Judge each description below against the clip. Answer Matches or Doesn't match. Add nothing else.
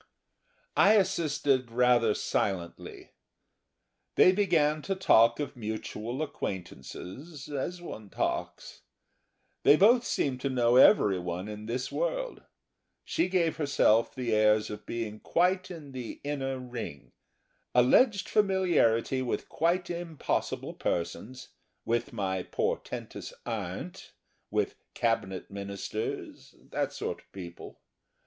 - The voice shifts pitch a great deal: Matches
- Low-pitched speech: Matches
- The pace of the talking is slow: Matches